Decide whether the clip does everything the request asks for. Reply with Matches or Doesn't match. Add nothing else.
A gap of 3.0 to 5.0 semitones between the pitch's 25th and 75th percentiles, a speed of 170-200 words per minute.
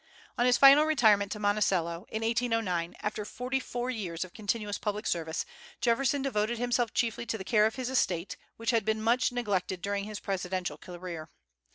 Matches